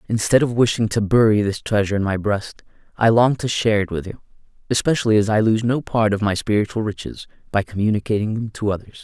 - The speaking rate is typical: No, fast, 215 wpm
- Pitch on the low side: Yes, low, 110 Hz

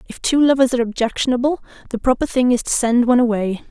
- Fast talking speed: Yes, fast, 210 wpm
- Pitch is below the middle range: No, high, 245 Hz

